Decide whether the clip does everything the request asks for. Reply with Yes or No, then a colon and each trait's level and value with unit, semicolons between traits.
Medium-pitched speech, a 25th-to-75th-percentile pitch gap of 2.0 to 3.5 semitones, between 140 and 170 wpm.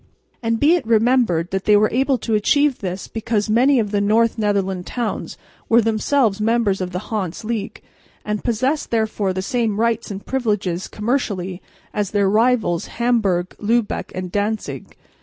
No: high, 215 Hz; average, 3.1 semitones; average, 160 wpm